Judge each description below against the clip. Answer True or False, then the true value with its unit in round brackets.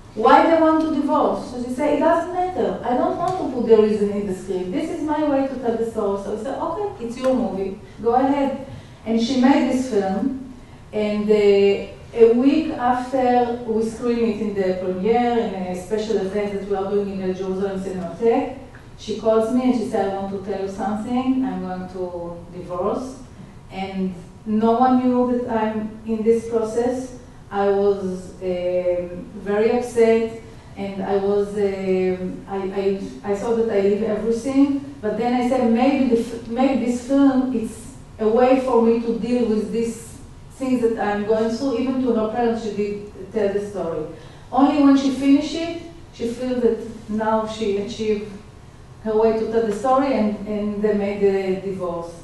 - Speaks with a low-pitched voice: False (225 Hz)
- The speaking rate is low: False (190 wpm)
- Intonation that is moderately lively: True (3.9 semitones)